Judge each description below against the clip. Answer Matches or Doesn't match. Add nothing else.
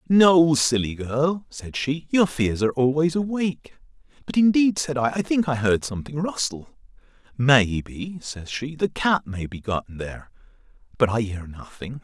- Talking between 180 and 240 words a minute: Doesn't match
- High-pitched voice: Doesn't match